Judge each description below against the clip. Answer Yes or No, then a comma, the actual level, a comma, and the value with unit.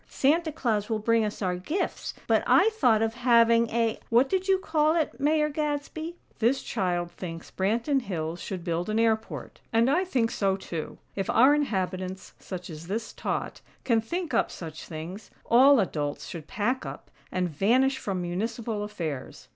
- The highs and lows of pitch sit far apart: Yes, wide, 6.5 semitones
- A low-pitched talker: No, high, 225 Hz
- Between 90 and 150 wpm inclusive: No, average, 170 wpm